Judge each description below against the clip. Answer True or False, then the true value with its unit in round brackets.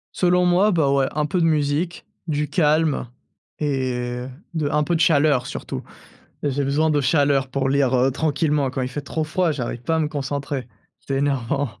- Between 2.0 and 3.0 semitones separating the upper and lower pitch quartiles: True (2.6 semitones)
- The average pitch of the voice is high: False (145 Hz)